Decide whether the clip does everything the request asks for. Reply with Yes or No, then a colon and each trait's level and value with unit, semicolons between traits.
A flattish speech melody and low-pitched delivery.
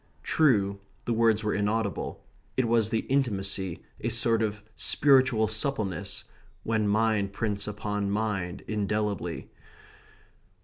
Yes: narrow, 2.1 semitones; low, 105 Hz